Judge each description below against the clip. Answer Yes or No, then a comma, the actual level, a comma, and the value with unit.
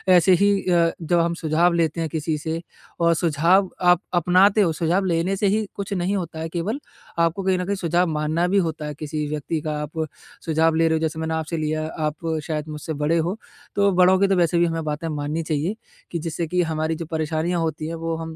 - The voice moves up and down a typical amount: No, narrow, 2.1 semitones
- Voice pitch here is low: No, medium, 165 Hz